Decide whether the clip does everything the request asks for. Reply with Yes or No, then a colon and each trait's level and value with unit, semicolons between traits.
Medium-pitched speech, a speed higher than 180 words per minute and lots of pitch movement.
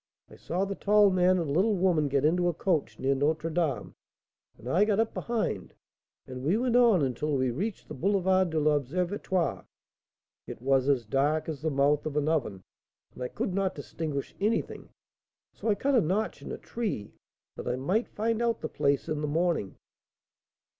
Yes: medium, 165 Hz; average, 190 wpm; wide, 5.9 semitones